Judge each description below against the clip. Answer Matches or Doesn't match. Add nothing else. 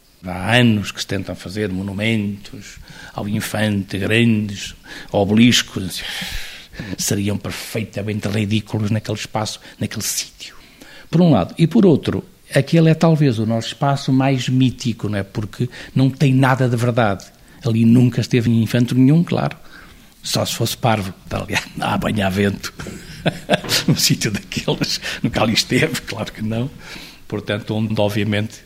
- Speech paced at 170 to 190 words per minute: Doesn't match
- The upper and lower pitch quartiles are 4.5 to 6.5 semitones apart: Doesn't match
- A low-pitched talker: Matches